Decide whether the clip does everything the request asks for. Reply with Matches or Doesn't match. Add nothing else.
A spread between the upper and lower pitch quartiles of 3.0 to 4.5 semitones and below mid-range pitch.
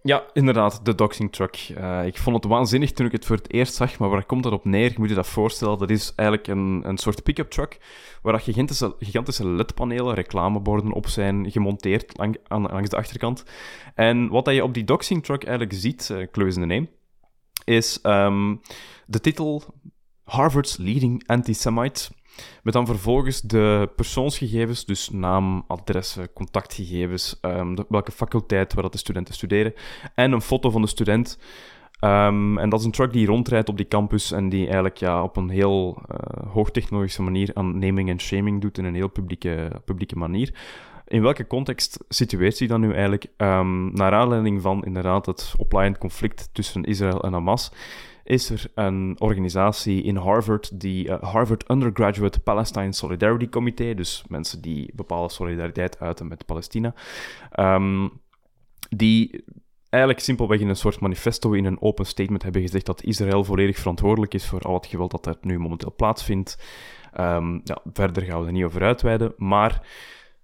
Matches